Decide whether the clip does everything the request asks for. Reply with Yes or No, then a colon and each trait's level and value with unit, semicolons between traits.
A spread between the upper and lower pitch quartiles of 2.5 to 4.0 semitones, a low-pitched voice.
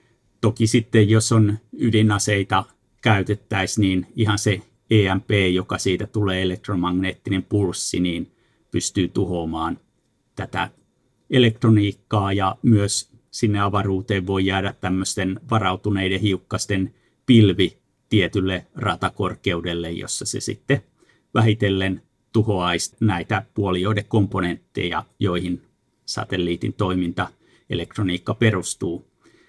Yes: average, 2.8 semitones; low, 100 Hz